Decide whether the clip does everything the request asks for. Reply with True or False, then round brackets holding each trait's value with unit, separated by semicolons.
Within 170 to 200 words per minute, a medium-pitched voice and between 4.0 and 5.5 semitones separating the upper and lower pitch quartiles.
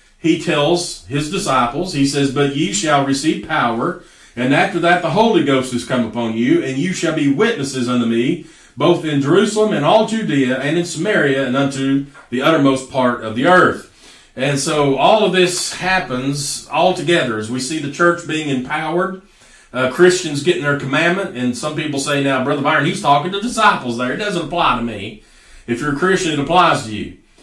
True (195 wpm; 145 Hz; 4.7 semitones)